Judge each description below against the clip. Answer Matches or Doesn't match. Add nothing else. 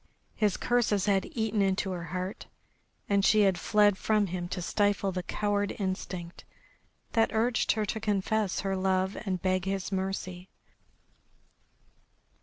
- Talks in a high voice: Matches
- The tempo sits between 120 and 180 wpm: Matches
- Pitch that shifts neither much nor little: Doesn't match